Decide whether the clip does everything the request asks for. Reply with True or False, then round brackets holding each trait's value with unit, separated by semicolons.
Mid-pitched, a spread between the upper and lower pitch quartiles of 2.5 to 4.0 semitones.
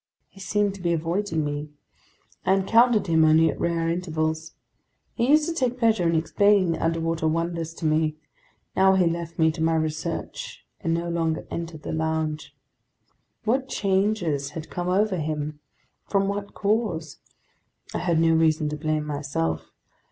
True (165 Hz; 3.6 semitones)